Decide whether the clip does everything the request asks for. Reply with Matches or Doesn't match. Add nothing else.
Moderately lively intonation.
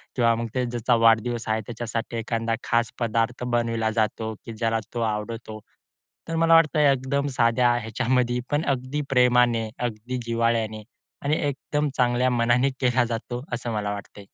Doesn't match